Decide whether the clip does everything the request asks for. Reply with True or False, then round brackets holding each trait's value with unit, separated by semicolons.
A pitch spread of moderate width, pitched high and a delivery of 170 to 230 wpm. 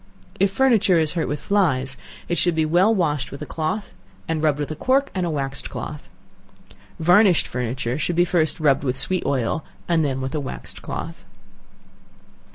False (4.4 semitones; 155 Hz; 180 wpm)